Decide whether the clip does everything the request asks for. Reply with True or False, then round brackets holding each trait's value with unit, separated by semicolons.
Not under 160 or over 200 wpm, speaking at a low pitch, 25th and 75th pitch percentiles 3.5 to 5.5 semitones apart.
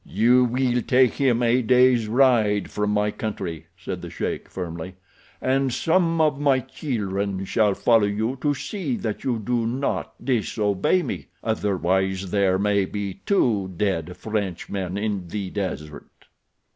False (140 wpm; 105 Hz; 4.6 semitones)